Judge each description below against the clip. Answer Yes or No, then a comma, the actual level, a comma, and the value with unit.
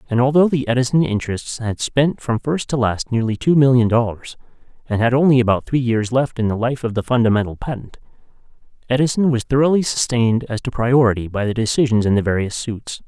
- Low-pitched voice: Yes, low, 120 Hz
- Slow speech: No, average, 195 wpm